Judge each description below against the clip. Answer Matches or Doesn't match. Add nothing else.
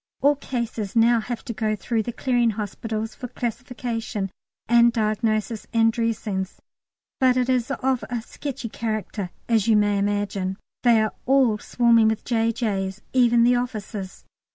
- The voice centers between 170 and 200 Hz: Doesn't match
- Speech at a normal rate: Matches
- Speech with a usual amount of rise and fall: Doesn't match